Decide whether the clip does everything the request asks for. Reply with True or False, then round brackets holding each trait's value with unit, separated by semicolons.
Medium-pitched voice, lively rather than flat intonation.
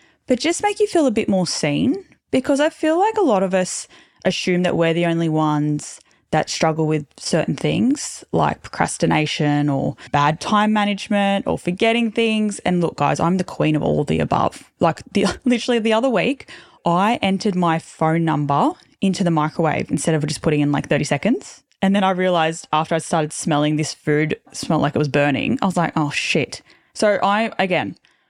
True (175 Hz; 5.9 semitones)